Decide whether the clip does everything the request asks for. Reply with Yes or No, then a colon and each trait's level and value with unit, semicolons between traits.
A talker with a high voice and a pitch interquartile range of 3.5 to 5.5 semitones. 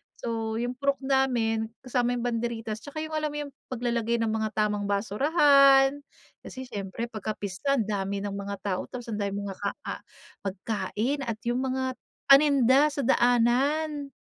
Yes: high, 235 Hz; average, 4.2 semitones